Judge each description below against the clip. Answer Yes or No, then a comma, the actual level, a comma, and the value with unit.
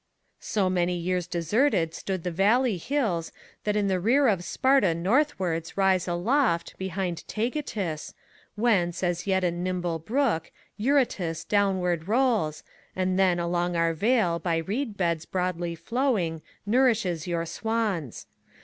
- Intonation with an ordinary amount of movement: Yes, average, 4.5 semitones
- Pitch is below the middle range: No, medium, 185 Hz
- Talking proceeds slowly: Yes, slow, 130 wpm